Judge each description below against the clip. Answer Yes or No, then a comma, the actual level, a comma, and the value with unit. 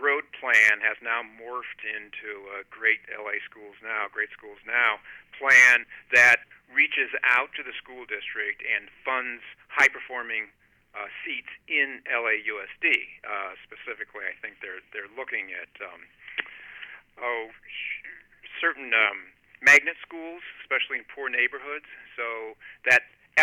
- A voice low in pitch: Yes, low, 115 Hz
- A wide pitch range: Yes, wide, 7.6 semitones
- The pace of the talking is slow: Yes, slow, 125 wpm